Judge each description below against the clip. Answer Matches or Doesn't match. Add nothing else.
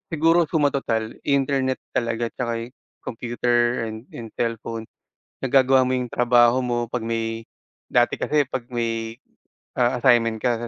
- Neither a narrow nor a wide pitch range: Doesn't match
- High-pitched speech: Doesn't match